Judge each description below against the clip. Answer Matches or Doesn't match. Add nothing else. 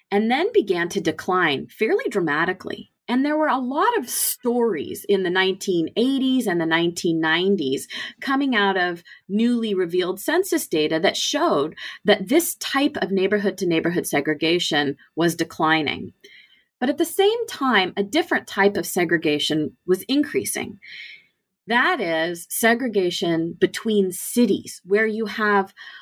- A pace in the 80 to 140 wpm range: Matches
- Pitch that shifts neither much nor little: Doesn't match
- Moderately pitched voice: Doesn't match